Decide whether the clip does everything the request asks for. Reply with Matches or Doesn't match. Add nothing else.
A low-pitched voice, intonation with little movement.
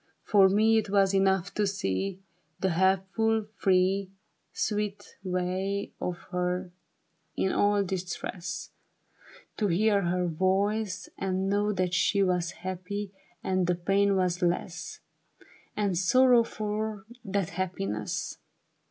Doesn't match